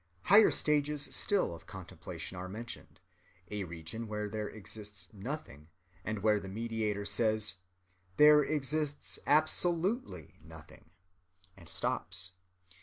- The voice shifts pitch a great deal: Yes, wide, 7.8 semitones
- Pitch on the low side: Yes, low, 105 Hz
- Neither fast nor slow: No, slow, 110 wpm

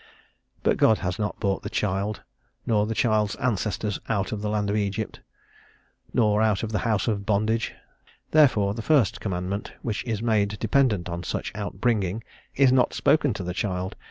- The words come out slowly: No, average, 180 wpm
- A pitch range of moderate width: No, narrow, 2.1 semitones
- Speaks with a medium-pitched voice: No, low, 105 Hz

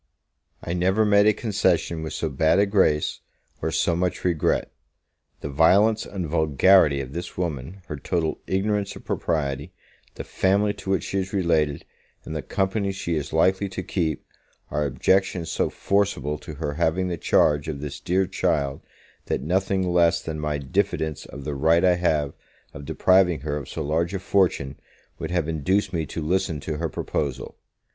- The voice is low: Yes, very low, 85 Hz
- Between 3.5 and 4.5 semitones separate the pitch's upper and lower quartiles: Yes, average, 4.0 semitones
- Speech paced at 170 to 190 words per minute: Yes, average, 175 wpm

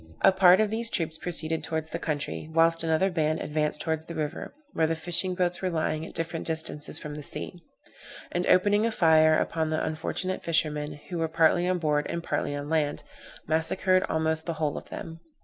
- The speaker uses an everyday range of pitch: No, narrow, 2.0 semitones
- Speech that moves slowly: No, average, 200 wpm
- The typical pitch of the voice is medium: Yes, medium, 160 Hz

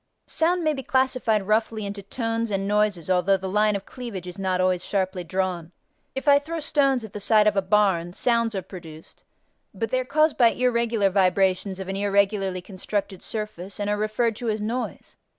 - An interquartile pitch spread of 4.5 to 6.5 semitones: No, average, 3.4 semitones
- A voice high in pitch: Yes, high, 205 Hz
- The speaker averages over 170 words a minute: Yes, average, 195 wpm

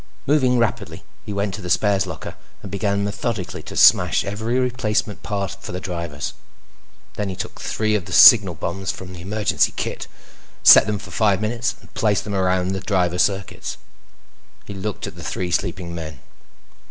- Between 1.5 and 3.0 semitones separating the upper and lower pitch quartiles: Yes, average, 2.7 semitones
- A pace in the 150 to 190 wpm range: Yes, average, 175 wpm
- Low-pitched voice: Yes, low, 100 Hz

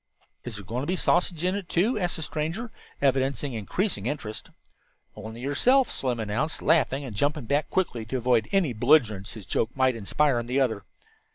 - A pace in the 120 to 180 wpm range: No, average, 190 wpm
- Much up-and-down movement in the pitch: Yes, wide, 5.9 semitones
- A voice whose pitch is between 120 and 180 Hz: Yes, low, 135 Hz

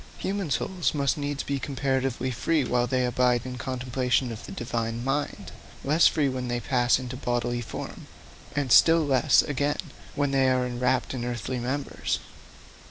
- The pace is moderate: Yes, average, 165 wpm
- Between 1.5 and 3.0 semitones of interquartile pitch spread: Yes, narrow, 2.4 semitones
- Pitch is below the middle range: Yes, low, 130 Hz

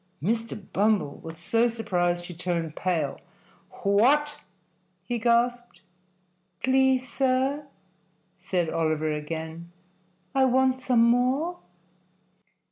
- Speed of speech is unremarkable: No, slow, 95 wpm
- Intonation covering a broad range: Yes, wide, 6.9 semitones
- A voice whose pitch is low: No, high, 225 Hz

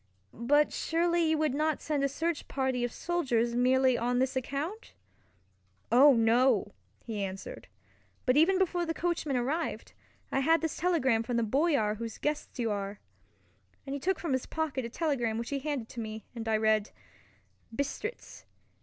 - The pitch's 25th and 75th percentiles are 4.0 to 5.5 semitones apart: Yes, average, 5.2 semitones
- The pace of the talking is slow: No, average, 170 wpm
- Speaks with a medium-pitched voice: No, very high, 265 Hz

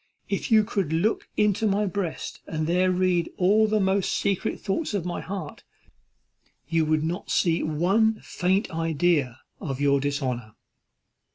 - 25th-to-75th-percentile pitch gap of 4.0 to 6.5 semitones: Yes, average, 4.3 semitones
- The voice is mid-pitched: Yes, medium, 180 Hz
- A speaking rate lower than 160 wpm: Yes, average, 150 wpm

